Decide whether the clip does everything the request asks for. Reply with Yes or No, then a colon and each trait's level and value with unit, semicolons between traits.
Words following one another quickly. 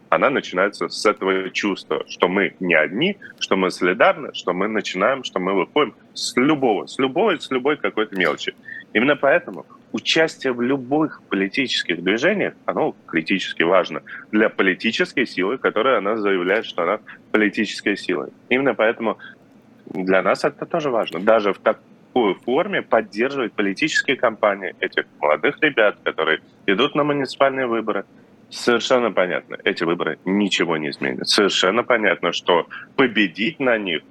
No: average, 145 wpm